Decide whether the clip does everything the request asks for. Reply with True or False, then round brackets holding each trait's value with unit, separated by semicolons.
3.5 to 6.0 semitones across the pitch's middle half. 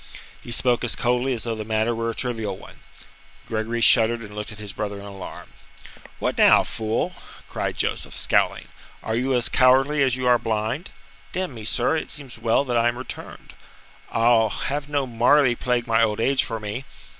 False (2.5 semitones)